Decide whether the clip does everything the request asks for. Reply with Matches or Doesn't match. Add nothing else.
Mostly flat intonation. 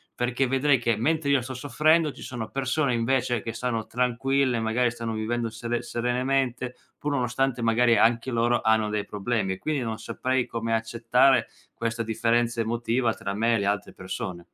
Matches